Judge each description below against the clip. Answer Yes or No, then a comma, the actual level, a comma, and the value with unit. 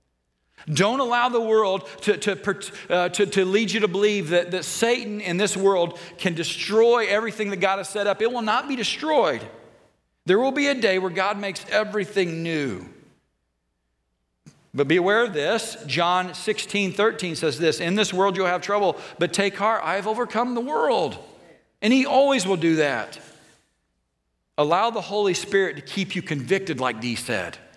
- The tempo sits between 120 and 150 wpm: No, average, 175 wpm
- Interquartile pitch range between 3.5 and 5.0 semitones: Yes, average, 4.2 semitones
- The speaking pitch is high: Yes, high, 195 Hz